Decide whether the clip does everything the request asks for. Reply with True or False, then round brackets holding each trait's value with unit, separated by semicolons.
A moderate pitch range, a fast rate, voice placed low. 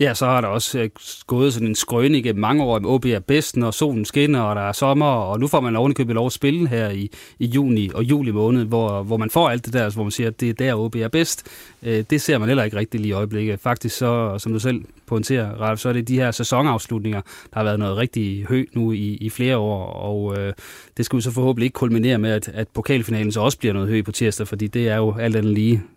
True (3.1 semitones; 250 wpm; 115 Hz)